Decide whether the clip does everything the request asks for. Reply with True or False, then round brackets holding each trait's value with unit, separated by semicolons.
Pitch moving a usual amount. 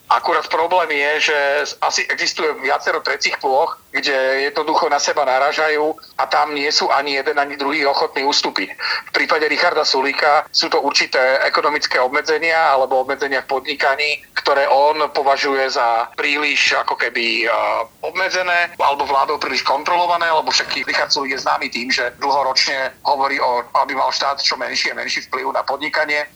False (2.2 semitones)